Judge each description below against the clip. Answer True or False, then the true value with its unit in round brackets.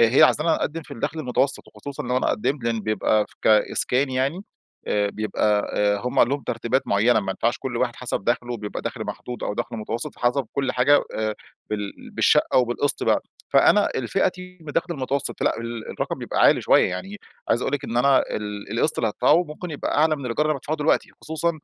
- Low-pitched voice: True (125 Hz)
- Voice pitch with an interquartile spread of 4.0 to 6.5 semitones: True (4.6 semitones)